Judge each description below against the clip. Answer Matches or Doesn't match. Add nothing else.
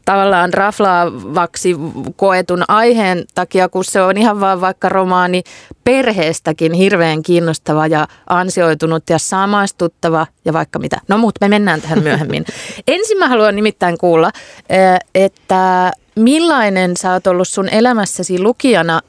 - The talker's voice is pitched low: Doesn't match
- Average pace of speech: Matches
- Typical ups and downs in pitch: Matches